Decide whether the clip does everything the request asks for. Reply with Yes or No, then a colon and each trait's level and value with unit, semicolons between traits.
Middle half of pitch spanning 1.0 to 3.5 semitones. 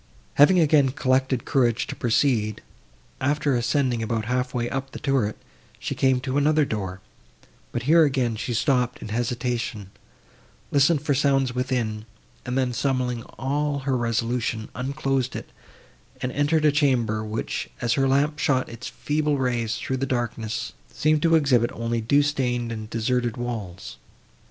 Yes: average, 3.2 semitones